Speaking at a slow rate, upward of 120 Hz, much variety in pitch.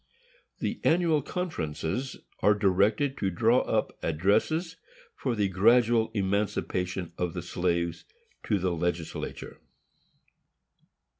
No: slow, 100 wpm; low, 100 Hz; wide, 5.7 semitones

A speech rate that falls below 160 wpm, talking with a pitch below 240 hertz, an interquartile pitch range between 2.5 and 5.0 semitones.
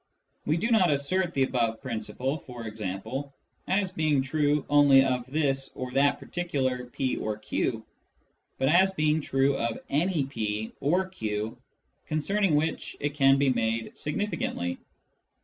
Yes: average, 145 wpm; medium, 140 Hz; average, 3.8 semitones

